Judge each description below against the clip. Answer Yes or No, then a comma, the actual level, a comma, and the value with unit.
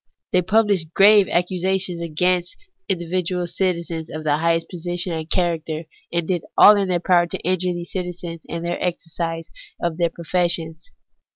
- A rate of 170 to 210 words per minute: No, average, 155 wpm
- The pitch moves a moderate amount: No, narrow, 1.6 semitones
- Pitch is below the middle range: No, medium, 175 Hz